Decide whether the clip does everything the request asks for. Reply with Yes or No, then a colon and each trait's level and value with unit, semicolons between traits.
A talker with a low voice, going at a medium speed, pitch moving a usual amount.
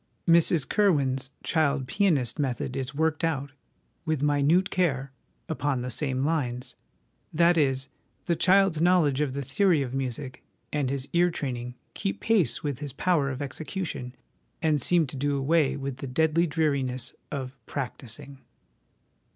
No: medium, 145 Hz; average, 150 wpm; average, 3.6 semitones